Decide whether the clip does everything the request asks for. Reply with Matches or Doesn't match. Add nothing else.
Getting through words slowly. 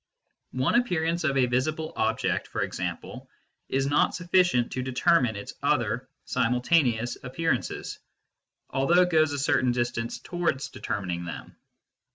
Matches